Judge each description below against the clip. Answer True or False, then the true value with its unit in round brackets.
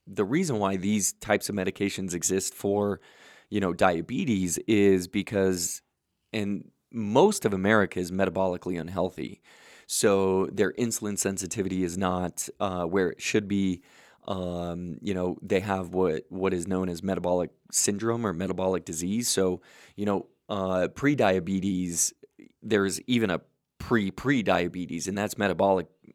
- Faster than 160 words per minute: False (140 wpm)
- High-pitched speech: False (95 Hz)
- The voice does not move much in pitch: True (2.1 semitones)